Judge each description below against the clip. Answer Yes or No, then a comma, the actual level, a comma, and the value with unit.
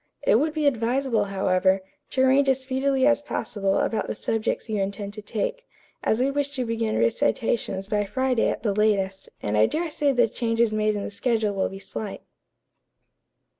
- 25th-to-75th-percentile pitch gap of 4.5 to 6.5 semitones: Yes, average, 4.8 semitones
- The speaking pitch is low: No, high, 225 Hz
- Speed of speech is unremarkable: Yes, average, 185 wpm